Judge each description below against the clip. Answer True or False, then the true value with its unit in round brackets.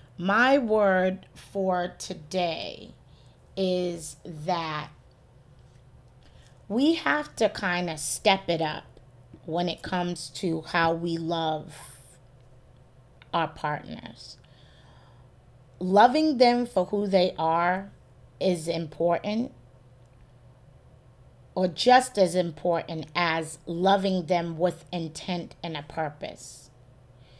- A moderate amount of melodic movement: False (5.7 semitones)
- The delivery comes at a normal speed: False (95 wpm)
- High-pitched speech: False (170 Hz)